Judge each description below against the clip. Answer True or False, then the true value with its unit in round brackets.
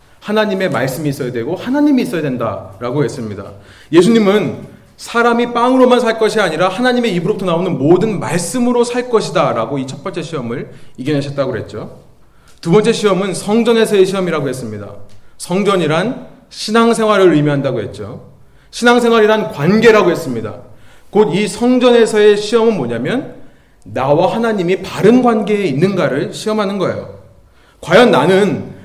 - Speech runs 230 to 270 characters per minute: False (360 characters per minute)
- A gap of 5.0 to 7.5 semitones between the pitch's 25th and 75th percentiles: False (7.9 semitones)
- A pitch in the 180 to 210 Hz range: True (190 Hz)